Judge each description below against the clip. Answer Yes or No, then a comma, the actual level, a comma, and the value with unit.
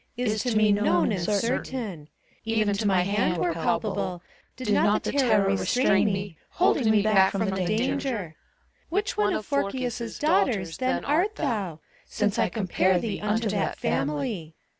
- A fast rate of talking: No, average, 160 wpm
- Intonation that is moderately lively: Yes, average, 3.7 semitones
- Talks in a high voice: Yes, high, 210 Hz